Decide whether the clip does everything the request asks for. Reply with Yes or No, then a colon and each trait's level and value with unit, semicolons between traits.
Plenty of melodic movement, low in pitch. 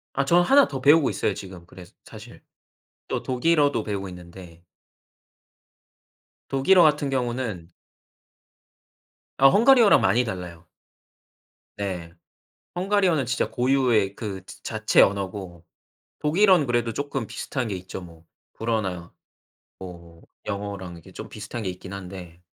Yes: wide, 7.0 semitones; low, 110 Hz